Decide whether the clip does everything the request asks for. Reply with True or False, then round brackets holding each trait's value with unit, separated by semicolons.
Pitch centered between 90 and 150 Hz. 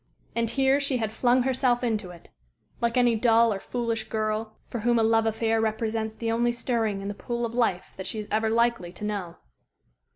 False (225 Hz)